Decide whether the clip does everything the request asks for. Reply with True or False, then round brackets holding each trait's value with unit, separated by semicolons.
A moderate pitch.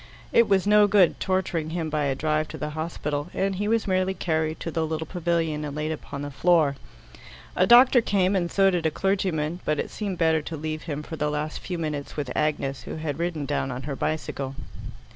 True (160 Hz)